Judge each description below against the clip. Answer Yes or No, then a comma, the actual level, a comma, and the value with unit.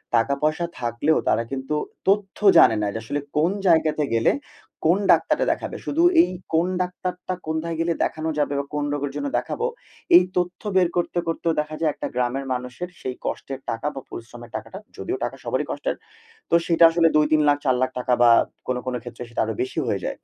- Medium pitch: Yes, medium, 155 Hz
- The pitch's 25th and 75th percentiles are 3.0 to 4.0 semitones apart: No, average, 5.1 semitones